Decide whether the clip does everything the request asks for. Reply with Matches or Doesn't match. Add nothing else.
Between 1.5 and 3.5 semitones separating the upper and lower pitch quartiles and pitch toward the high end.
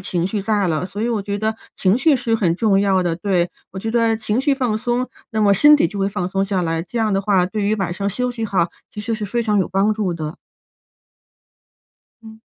Matches